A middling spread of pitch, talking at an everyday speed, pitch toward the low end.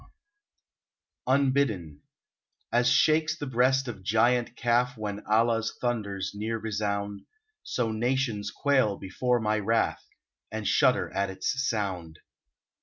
No: average, 3.5 semitones; slow, 120 wpm; low, 115 Hz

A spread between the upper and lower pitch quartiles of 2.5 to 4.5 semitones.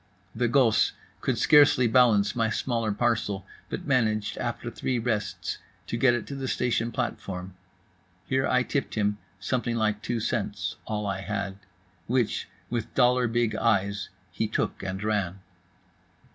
Yes: average, 3.0 semitones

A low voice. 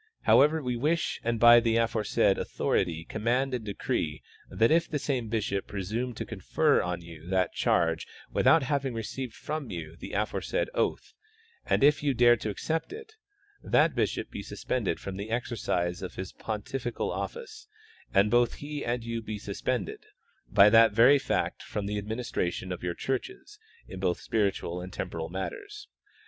Yes: low, 115 Hz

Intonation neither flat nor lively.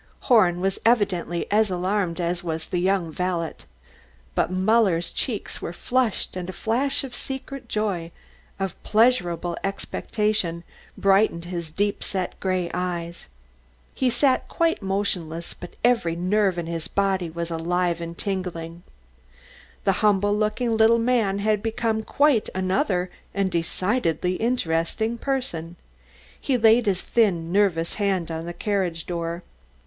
Yes: average, 4.1 semitones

